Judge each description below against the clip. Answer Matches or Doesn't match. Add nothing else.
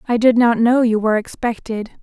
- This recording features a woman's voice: Matches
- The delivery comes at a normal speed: Doesn't match